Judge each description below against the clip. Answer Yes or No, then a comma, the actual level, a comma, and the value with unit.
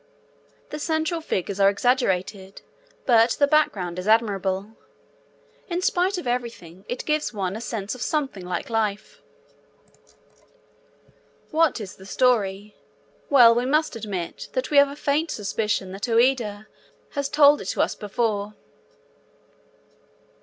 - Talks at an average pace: No, slow, 130 wpm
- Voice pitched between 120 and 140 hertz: No, high, 230 Hz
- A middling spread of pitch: No, wide, 6.1 semitones